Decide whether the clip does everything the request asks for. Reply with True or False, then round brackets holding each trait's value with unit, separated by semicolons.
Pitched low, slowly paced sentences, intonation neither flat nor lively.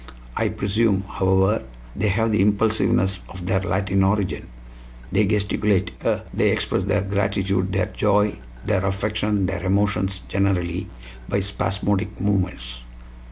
False (100 Hz; 125 wpm; 1.4 semitones)